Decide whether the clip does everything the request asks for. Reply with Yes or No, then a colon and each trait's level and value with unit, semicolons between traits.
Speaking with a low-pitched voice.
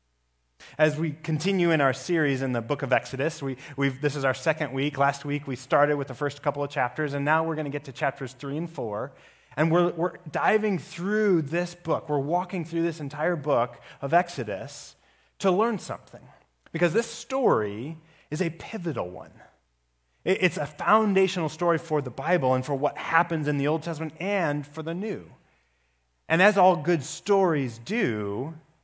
No: medium, 155 Hz